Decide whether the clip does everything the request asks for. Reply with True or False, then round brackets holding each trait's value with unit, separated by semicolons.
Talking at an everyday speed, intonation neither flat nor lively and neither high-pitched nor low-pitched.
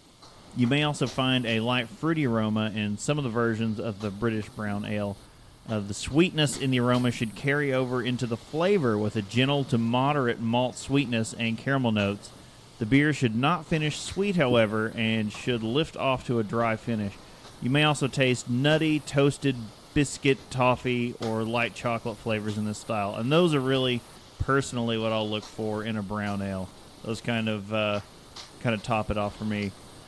False (190 wpm; 3.6 semitones; 120 Hz)